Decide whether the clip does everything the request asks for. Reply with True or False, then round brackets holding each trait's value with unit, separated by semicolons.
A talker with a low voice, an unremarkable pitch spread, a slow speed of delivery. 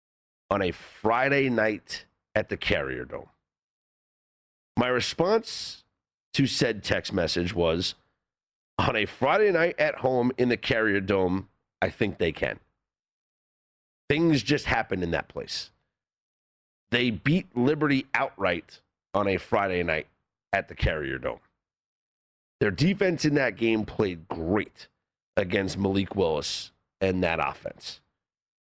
False (110 Hz; 7.5 semitones; 125 wpm)